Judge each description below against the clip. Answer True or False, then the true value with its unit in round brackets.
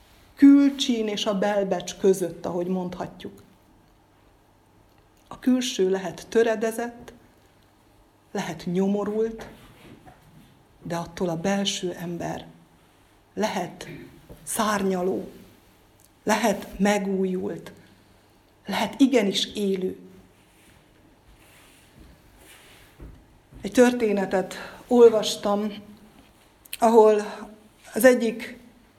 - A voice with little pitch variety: False (3.9 semitones)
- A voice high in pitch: True (200 Hz)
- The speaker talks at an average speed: False (65 wpm)